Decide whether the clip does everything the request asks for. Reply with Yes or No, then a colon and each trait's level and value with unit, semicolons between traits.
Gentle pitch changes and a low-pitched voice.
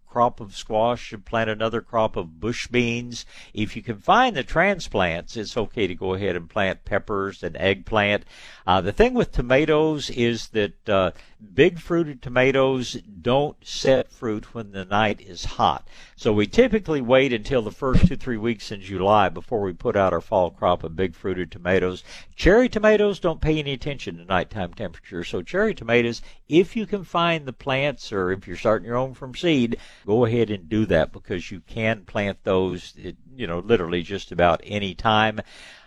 No: average, 5.2 semitones; low, 115 Hz